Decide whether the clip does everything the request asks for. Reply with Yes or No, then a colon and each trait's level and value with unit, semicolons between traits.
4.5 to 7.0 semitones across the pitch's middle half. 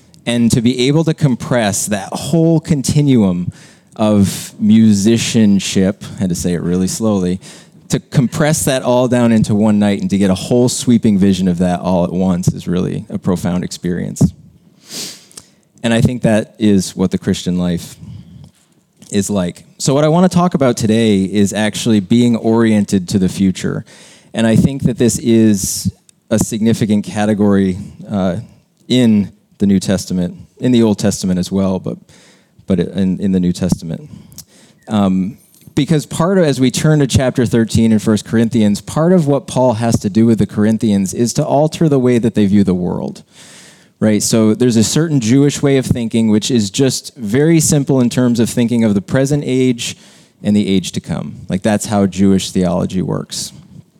Yes: average, 4.8 semitones